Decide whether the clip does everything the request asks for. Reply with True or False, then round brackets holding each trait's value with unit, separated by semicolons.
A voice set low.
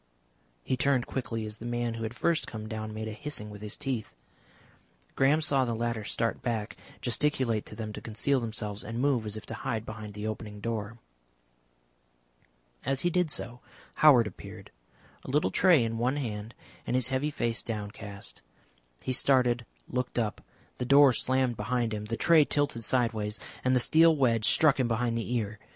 True (120 Hz)